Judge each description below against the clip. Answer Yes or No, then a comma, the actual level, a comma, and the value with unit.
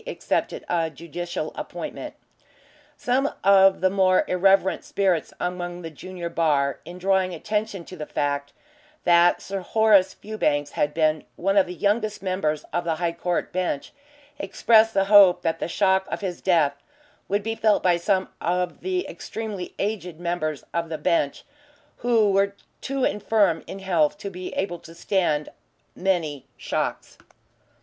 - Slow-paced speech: No, average, 155 wpm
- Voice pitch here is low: No, medium, 180 Hz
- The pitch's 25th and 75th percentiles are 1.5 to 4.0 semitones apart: Yes, average, 3.0 semitones